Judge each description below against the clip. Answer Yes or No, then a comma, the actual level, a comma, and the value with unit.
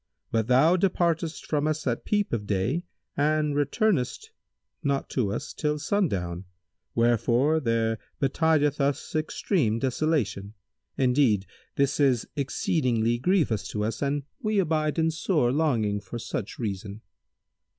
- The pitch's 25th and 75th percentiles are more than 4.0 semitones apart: Yes, wide, 5.6 semitones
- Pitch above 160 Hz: No, medium, 140 Hz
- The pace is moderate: No, slow, 130 wpm